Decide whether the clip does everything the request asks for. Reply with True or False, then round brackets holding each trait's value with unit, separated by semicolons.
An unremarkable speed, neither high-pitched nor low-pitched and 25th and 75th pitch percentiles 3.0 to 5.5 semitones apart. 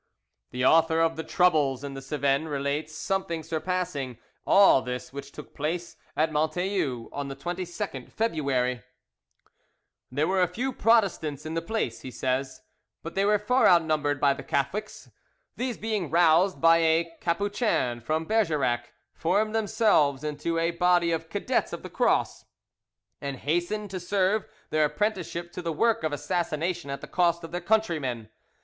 True (155 wpm; 165 Hz; 4.5 semitones)